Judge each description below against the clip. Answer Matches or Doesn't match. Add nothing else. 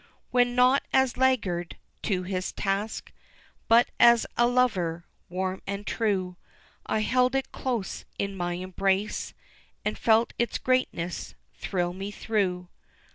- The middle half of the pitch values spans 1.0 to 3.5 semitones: Doesn't match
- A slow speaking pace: Matches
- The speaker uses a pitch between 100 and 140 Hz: Doesn't match